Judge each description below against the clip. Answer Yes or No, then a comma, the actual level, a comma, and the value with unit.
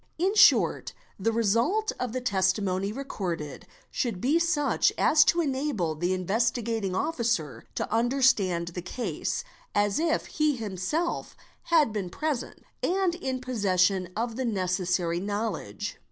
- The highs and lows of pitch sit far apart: Yes, wide, 6.6 semitones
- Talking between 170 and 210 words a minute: No, average, 140 wpm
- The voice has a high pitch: Yes, high, 225 Hz